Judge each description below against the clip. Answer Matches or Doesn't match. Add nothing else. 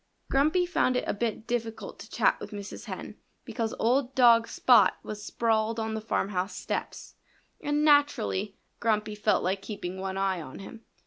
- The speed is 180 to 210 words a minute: Doesn't match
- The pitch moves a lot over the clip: Doesn't match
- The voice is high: Matches